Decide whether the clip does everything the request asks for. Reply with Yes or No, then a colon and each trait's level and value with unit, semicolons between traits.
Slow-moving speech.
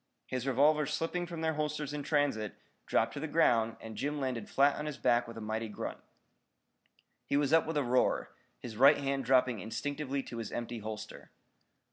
No: average, 190 wpm